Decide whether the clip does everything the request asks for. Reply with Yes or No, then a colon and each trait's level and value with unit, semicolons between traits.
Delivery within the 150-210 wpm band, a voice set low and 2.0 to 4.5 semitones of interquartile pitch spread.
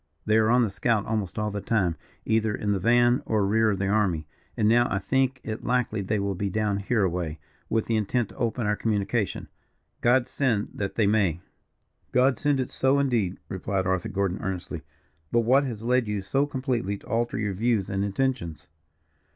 Yes: average, 200 wpm; low, 110 Hz; average, 3.5 semitones